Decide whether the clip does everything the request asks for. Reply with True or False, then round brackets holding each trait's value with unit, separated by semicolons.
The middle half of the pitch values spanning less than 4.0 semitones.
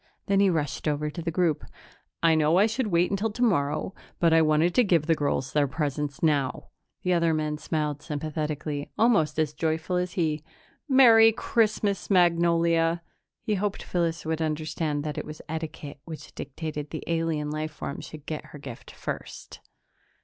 True (2.7 semitones)